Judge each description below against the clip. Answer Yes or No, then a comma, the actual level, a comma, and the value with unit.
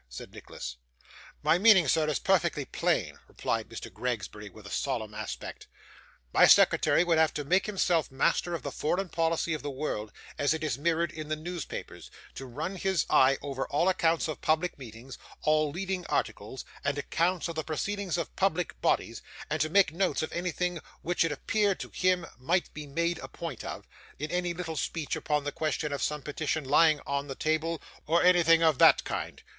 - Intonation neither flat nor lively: Yes, average, 3.6 semitones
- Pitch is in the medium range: Yes, medium, 160 Hz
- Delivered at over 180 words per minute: Yes, average, 190 wpm